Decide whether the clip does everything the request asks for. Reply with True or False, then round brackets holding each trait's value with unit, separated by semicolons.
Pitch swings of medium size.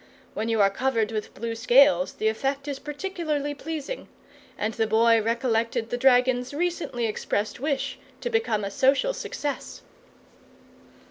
True (4.4 semitones)